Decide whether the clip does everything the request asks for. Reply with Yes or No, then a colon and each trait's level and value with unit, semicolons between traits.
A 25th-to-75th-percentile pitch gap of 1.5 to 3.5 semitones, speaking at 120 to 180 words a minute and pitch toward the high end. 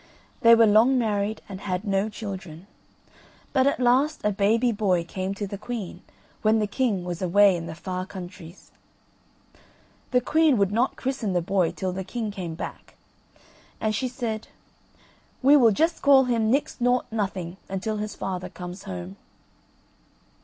No: average, 4.3 semitones; average, 160 wpm; high, 205 Hz